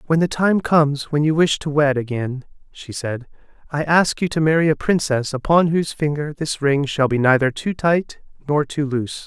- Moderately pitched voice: Yes, medium, 150 Hz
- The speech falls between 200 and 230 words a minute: Yes, fast, 205 wpm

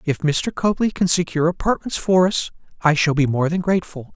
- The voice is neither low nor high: Yes, medium, 170 Hz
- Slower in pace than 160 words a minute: No, average, 200 wpm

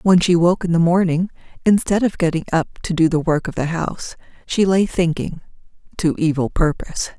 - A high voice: No, medium, 170 Hz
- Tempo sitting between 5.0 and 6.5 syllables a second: Yes, 5.5 syllables/s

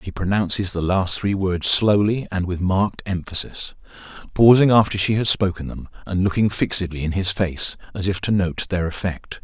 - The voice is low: Yes, very low, 95 Hz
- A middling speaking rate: Yes, average, 185 wpm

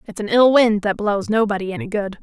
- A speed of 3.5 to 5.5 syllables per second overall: No, 5.7 syllables/s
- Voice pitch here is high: Yes, high, 210 Hz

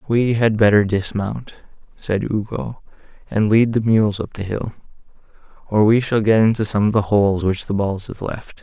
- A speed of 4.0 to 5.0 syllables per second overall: Yes, 4.8 syllables/s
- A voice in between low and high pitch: No, low, 105 Hz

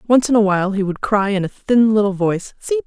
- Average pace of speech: No, fast, 270 wpm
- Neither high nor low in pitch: No, high, 210 Hz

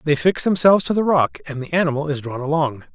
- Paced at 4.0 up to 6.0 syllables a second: No, 6.4 syllables/s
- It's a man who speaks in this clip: Yes, male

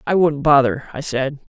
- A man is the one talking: Yes, male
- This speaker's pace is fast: No, average, 195 wpm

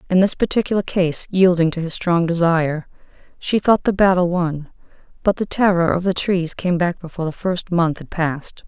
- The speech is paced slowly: No, average, 195 wpm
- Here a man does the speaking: No, female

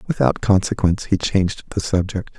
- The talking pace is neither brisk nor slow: Yes, average, 150 wpm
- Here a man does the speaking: Yes, male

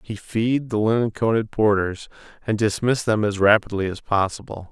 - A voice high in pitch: No, low, 105 Hz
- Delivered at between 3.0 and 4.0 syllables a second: No, 5.2 syllables/s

